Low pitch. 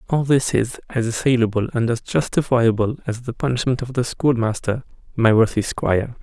Yes: low, 120 Hz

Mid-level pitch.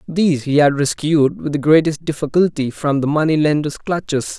Yes: medium, 150 Hz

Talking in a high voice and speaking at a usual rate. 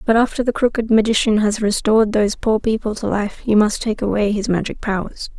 No: high, 215 Hz; fast, 210 wpm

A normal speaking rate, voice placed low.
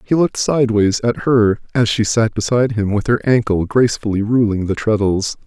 Yes: average, 185 wpm; low, 110 Hz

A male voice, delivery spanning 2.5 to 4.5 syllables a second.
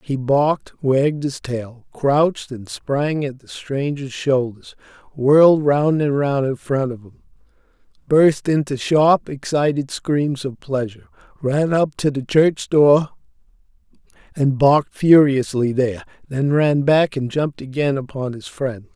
Yes: male; 4.1 syllables/s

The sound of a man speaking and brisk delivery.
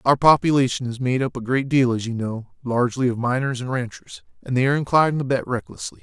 Yes: male; fast, 230 wpm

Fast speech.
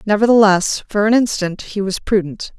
No: average, 165 wpm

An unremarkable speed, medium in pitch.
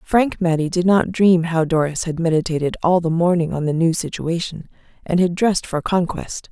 Yes: average, 195 wpm; medium, 170 Hz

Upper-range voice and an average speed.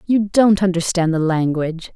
No: medium, 180 Hz; average, 155 wpm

